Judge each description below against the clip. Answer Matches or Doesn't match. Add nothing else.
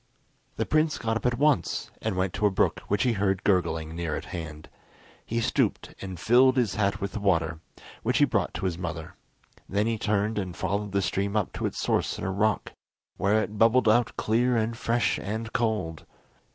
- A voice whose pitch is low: Matches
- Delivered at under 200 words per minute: Doesn't match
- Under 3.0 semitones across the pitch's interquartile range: Doesn't match